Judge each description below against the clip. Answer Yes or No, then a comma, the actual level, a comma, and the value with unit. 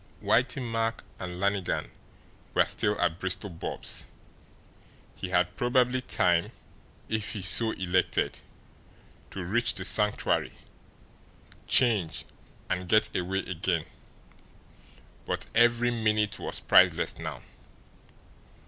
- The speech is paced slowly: Yes, slow, 105 wpm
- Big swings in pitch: No, average, 4.0 semitones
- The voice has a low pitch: Yes, low, 100 Hz